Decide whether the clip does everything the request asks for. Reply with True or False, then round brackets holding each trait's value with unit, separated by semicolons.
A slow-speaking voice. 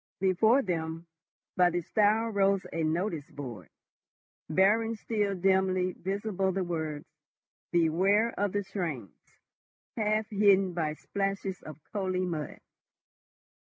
True (115 wpm)